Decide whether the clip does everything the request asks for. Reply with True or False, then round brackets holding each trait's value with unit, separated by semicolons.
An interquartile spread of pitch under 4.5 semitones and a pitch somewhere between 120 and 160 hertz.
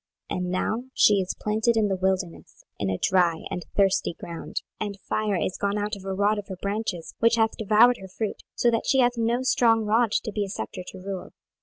False (2.9 semitones; 205 Hz)